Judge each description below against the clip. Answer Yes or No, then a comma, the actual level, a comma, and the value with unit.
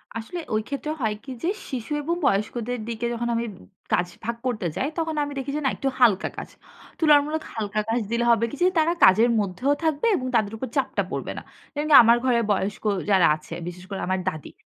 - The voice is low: No, high, 235 Hz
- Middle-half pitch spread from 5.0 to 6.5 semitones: Yes, average, 5.3 semitones